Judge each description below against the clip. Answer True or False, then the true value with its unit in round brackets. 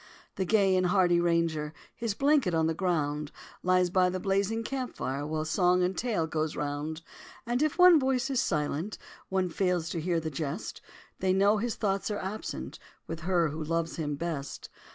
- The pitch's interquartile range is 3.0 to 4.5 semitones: True (4.2 semitones)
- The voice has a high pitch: False (180 Hz)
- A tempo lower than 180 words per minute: False (185 wpm)